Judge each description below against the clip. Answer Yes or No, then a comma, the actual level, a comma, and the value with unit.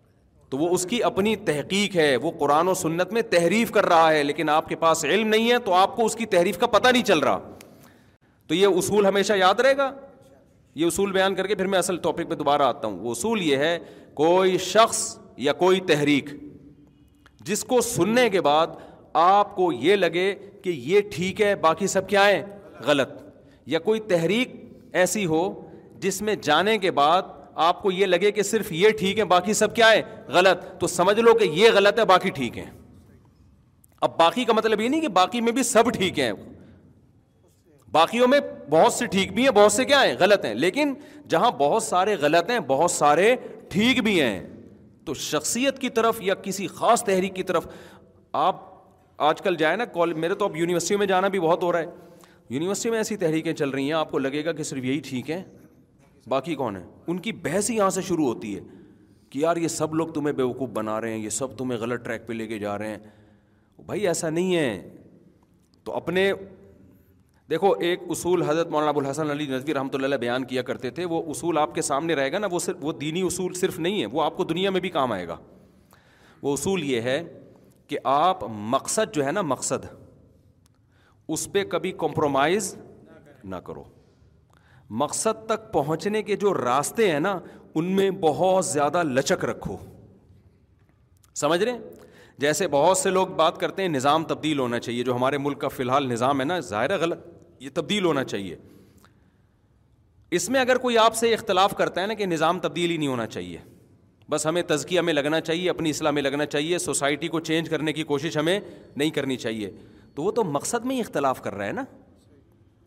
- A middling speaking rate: No, fast, 205 wpm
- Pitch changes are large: Yes, wide, 5.9 semitones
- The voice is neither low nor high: Yes, medium, 170 Hz